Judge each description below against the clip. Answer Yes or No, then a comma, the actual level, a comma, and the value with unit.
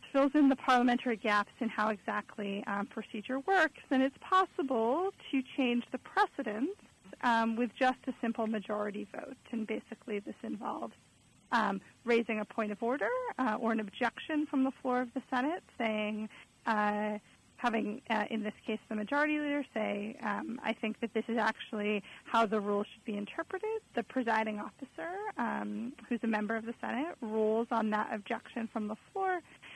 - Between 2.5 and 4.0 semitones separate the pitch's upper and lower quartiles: Yes, average, 3.6 semitones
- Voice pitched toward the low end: No, high, 230 Hz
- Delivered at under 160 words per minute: No, average, 175 wpm